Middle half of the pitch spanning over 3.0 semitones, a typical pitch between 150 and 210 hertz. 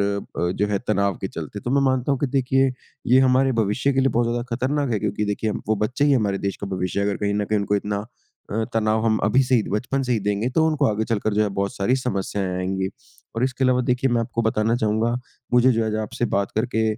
No: average, 3.7 semitones; low, 110 Hz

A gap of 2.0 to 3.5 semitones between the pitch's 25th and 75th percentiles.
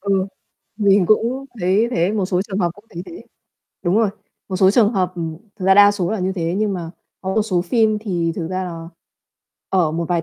Yes: average, 2.9 semitones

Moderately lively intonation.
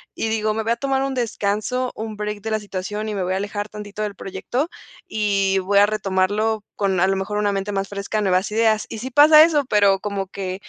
No: narrow, 2.0 semitones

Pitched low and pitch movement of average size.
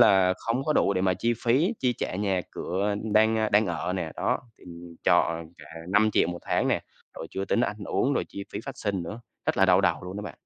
Yes: low, 100 Hz; average, 3.2 semitones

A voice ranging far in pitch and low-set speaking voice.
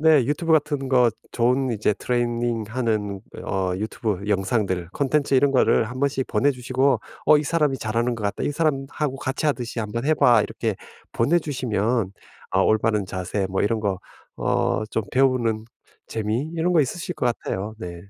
No: average, 4.3 semitones; low, 120 Hz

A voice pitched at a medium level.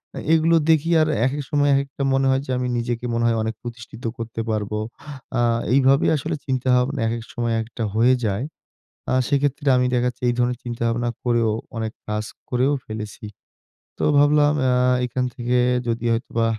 No: low, 125 Hz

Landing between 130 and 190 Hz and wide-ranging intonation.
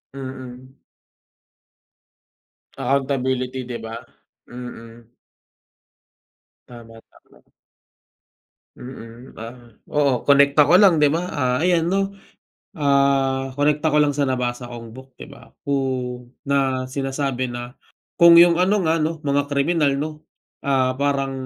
No: low, 135 Hz; average, 2.8 semitones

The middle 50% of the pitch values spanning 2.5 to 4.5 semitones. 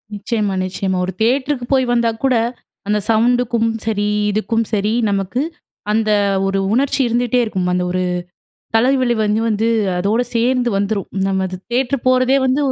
Yes: average, 3.5 semitones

